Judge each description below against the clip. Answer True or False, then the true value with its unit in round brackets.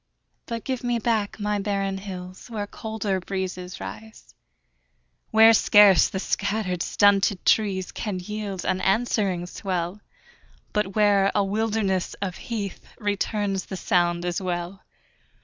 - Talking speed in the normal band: False (130 wpm)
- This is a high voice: True (195 Hz)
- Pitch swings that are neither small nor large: False (2.3 semitones)